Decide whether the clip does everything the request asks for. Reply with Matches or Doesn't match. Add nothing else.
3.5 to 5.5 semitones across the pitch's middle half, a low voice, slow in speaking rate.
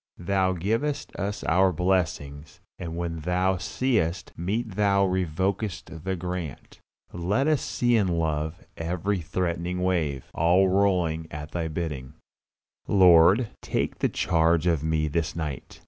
Doesn't match